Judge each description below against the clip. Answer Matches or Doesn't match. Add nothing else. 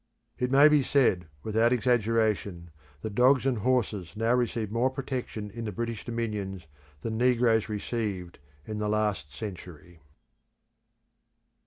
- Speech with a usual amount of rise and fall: Matches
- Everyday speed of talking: Doesn't match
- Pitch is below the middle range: Matches